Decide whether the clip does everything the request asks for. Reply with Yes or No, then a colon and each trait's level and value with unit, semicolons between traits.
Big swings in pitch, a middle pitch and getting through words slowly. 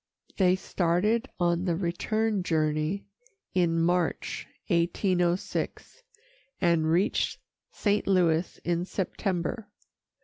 No: narrow, 2.5 semitones; medium, 175 Hz; slow, 90 wpm